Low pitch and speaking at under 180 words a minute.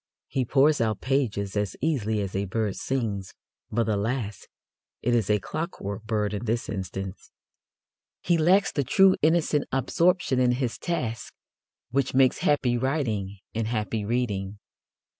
Yes: low, 115 Hz; average, 140 wpm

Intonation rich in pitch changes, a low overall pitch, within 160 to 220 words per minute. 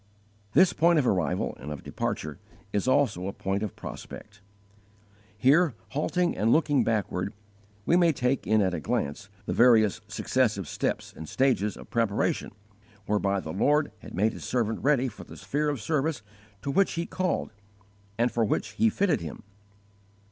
Yes: wide, 6.6 semitones; low, 115 Hz; average, 165 wpm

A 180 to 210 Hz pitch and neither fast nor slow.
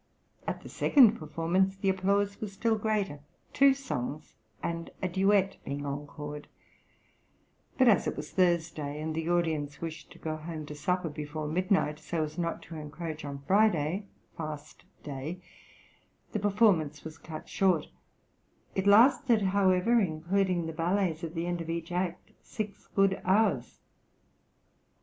No: medium, 170 Hz; average, 145 wpm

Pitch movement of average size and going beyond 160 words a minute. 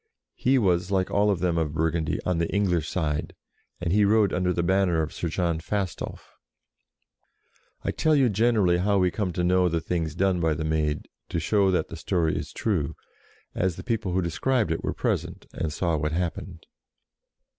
Yes: average, 3.2 semitones; average, 190 wpm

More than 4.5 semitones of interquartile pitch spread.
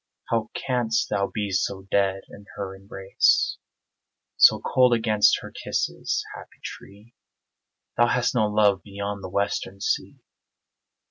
No: narrow, 2.4 semitones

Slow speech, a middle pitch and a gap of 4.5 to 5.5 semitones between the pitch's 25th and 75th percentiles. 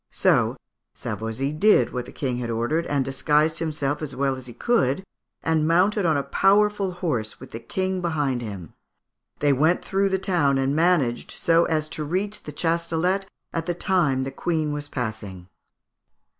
No: average, 170 wpm; medium, 155 Hz; average, 4.8 semitones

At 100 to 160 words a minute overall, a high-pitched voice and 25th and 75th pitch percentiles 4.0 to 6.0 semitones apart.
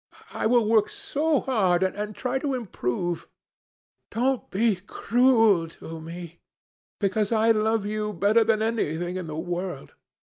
Yes: average, 140 wpm; high, 210 Hz; average, 4.4 semitones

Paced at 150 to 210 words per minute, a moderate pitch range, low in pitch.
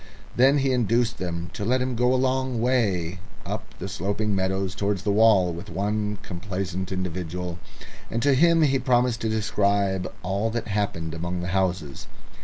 Yes: average, 170 wpm; average, 4.8 semitones; low, 100 Hz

